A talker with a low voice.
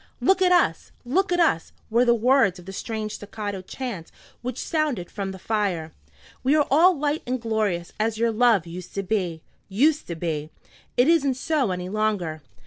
No: high, 220 Hz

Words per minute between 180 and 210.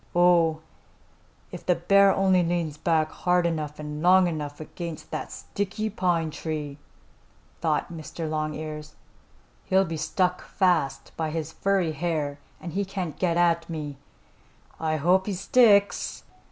No: slow, 135 wpm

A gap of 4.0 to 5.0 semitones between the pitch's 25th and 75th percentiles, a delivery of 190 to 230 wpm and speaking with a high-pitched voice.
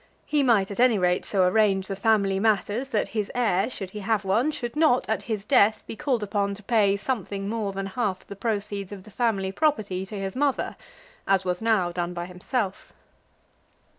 No: average, 2.9 semitones; average, 195 wpm; high, 205 Hz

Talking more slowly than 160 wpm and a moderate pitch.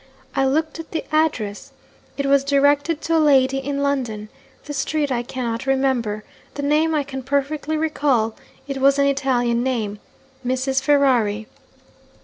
No: average, 150 wpm; very high, 275 Hz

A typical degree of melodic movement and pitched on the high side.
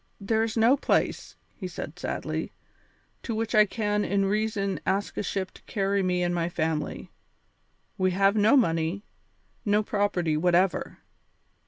Yes: average, 3.0 semitones; high, 200 Hz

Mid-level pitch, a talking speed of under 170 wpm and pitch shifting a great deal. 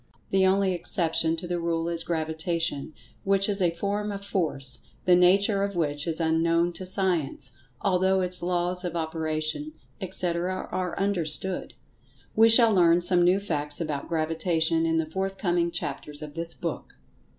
No: medium, 175 Hz; average, 155 wpm; average, 2.7 semitones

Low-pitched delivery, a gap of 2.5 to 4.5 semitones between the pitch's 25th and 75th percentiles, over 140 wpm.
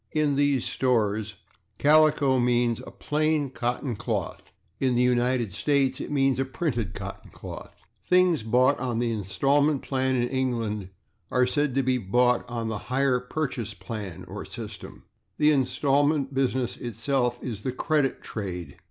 Yes: low, 125 Hz; average, 3.0 semitones; average, 150 wpm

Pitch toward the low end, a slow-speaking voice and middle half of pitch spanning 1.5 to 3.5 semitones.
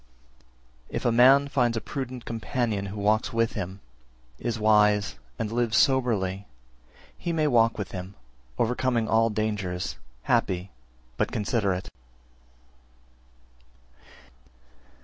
Yes: low, 110 Hz; slow, 110 wpm; average, 3.2 semitones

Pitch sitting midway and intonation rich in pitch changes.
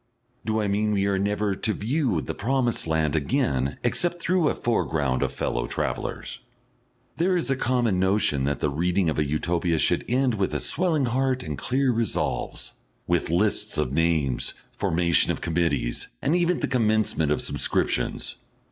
No: low, 100 Hz; wide, 7.7 semitones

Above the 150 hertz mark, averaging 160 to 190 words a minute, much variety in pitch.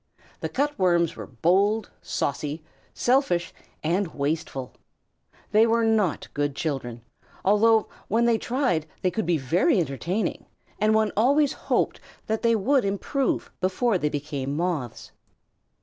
No: high, 190 Hz; slow, 135 wpm; wide, 6.6 semitones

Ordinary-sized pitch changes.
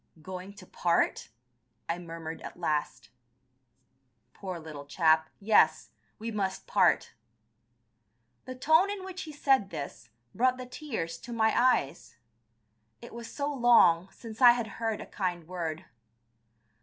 No: wide, 6.7 semitones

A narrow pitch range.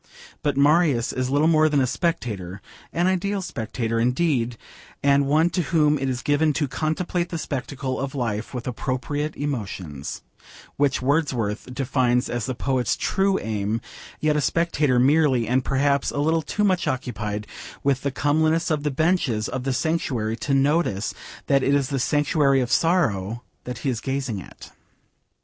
No: average, 4.1 semitones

